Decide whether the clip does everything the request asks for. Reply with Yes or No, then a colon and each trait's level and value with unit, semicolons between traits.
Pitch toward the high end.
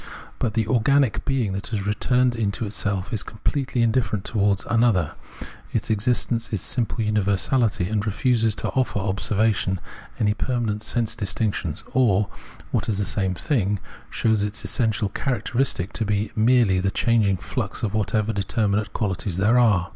No: low, 110 Hz